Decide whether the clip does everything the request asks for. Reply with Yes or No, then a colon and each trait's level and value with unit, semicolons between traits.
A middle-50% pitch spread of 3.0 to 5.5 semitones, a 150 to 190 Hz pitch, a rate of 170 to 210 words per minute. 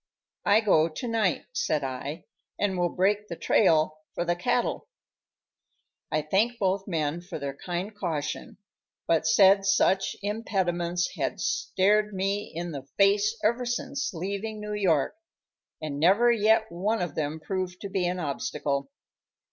No: average, 4.2 semitones; medium, 185 Hz; average, 150 wpm